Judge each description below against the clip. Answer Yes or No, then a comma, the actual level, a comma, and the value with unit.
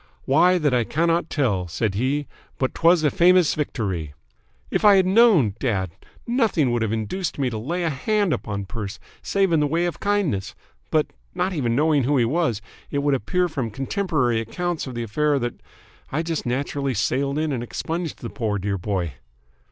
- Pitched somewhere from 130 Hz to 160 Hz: Yes, medium, 140 Hz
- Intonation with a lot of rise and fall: Yes, wide, 6.9 semitones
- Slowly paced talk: No, average, 190 wpm